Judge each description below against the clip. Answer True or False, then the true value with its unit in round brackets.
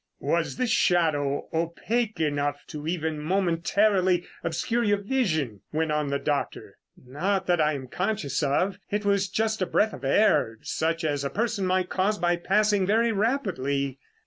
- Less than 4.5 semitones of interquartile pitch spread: False (5.5 semitones)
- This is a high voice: False (175 Hz)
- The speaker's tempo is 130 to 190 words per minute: True (160 wpm)